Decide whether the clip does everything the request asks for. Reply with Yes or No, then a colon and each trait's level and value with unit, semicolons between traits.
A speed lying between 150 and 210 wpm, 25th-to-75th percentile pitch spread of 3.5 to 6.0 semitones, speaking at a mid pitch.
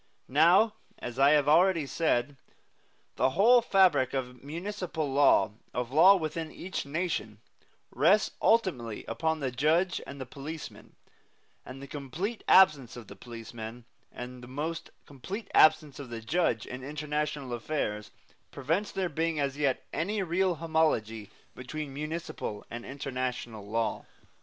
No: average, 140 wpm; average, 5.0 semitones; medium, 145 Hz